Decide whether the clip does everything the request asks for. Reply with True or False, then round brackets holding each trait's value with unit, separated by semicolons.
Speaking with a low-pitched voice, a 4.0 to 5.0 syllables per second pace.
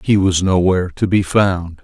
True (95 Hz; 4.7 syllables/s)